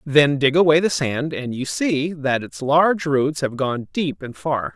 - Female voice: No, male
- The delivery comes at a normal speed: No, fast, 215 wpm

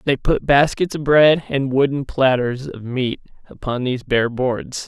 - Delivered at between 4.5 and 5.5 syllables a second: No, 4.3 syllables/s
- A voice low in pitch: Yes, low, 130 Hz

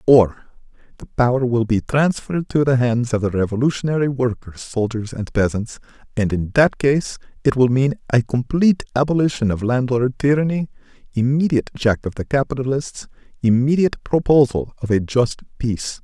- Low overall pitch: Yes, low, 125 Hz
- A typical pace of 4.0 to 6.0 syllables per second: Yes, 5.3 syllables/s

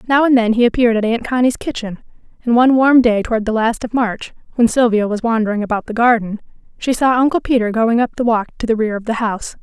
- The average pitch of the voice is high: Yes, high, 230 Hz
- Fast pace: Yes, fast, 245 wpm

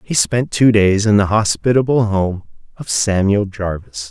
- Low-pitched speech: Yes, low, 100 Hz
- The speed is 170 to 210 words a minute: No, average, 160 wpm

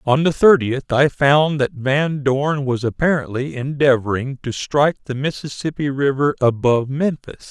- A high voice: No, low, 135 Hz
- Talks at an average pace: Yes, average, 145 wpm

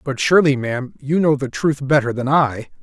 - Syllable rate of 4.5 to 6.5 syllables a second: Yes, 5.4 syllables/s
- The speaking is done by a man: Yes, male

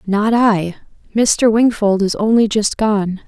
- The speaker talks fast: No, average, 145 wpm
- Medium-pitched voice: No, high, 210 Hz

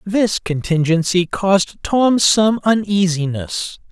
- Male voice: Yes, male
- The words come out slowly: Yes, slow, 90 wpm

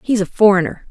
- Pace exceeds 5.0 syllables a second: Yes, 6.3 syllables/s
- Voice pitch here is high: Yes, high, 200 Hz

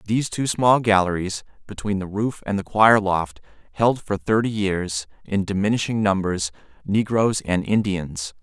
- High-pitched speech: No, low, 100 Hz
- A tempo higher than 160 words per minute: No, average, 150 wpm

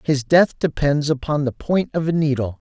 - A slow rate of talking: No, average, 200 wpm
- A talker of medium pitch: Yes, medium, 145 Hz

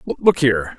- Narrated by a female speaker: No, male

